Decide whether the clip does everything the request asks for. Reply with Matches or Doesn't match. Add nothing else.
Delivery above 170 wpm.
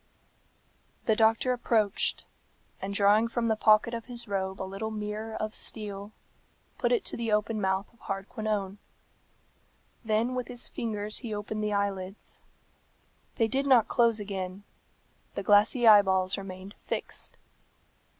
Doesn't match